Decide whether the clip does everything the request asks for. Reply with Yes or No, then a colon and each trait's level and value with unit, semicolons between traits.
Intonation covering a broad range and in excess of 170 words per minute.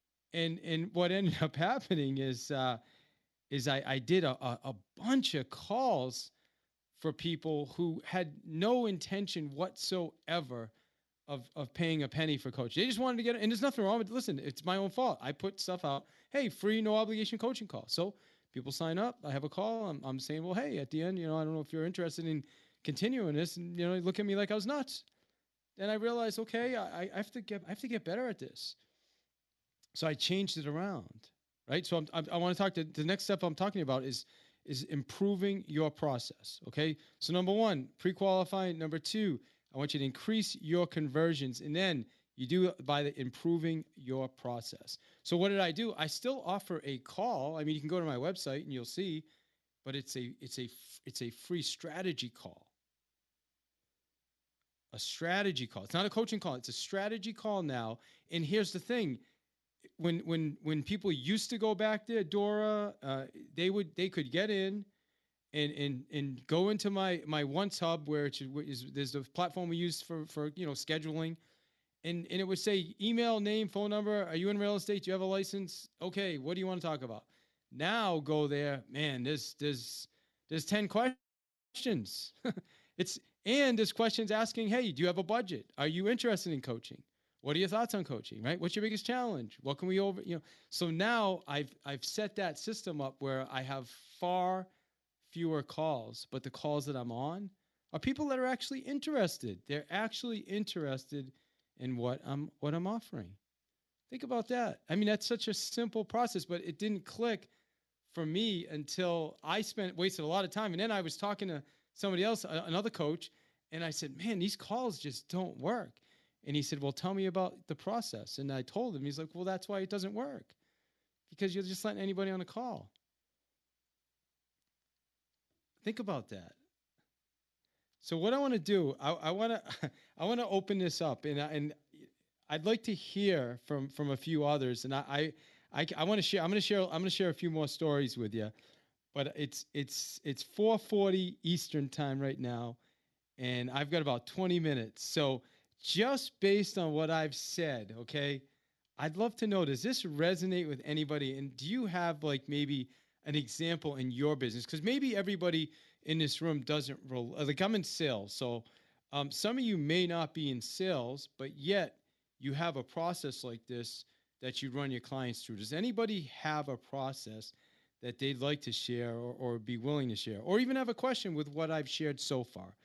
Yes: wide, 6.0 semitones; average, 200 wpm